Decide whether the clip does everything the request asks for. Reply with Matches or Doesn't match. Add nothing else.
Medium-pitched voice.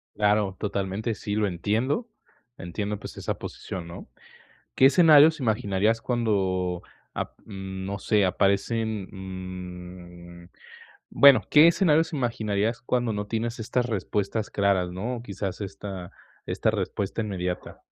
Doesn't match